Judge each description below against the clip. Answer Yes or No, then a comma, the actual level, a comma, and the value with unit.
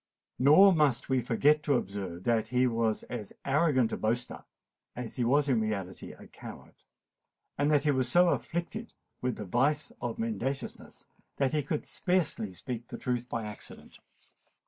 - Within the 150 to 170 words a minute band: Yes, average, 160 wpm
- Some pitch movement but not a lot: Yes, average, 4.7 semitones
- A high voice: No, low, 130 Hz